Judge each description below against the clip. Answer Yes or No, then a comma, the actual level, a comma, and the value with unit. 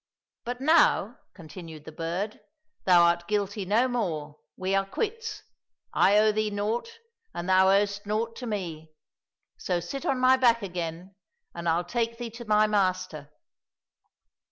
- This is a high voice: Yes, high, 205 Hz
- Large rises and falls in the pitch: No, average, 5.0 semitones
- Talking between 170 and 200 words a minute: No, average, 155 wpm